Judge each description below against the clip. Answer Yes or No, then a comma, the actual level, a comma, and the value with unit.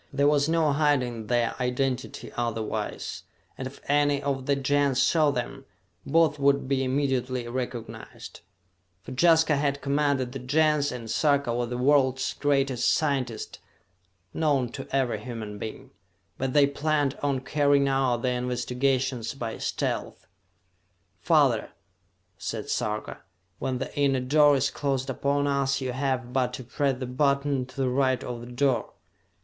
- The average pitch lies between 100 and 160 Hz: Yes, low, 135 Hz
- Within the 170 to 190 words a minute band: No, average, 145 wpm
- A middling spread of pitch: No, narrow, 2.2 semitones